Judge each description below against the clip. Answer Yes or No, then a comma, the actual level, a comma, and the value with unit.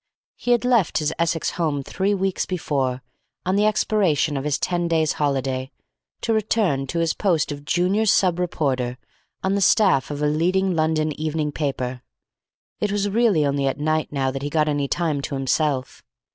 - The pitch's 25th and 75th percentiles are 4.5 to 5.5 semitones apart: Yes, average, 5.0 semitones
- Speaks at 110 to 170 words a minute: No, average, 180 wpm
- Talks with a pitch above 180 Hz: No, medium, 155 Hz